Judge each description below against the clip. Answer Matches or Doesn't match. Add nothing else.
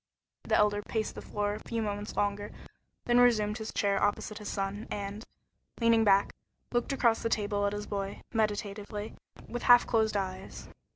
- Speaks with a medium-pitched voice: Doesn't match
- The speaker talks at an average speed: Matches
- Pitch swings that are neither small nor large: Doesn't match